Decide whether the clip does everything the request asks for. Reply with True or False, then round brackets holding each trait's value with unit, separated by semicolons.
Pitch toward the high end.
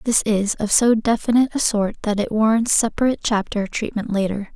True (220 Hz)